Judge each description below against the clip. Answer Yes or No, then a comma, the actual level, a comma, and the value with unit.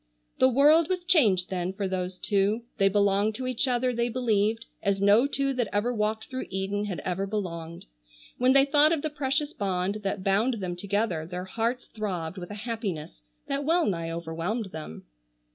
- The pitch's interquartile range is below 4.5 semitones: No, average, 5.2 semitones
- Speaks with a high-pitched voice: Yes, high, 210 Hz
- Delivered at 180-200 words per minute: Yes, average, 185 wpm